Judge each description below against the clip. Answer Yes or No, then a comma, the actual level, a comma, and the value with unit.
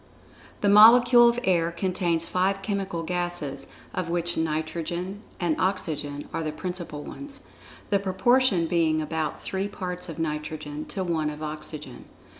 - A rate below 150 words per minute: Yes, average, 140 wpm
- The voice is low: No, medium, 175 Hz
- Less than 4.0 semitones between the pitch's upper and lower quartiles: Yes, average, 3.5 semitones